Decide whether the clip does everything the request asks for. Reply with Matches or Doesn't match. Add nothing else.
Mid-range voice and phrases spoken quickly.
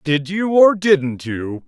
Doesn't match